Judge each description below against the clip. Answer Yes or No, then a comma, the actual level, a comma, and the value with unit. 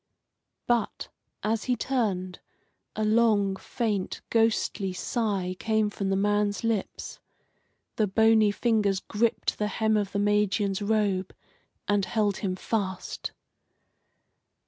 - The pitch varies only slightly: Yes, narrow, 2.1 semitones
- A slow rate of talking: Yes, slow, 115 wpm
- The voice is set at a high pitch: Yes, high, 210 Hz